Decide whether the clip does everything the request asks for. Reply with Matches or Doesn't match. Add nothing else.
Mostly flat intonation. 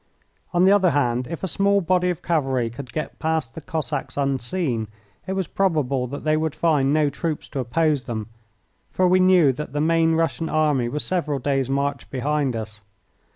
Doesn't match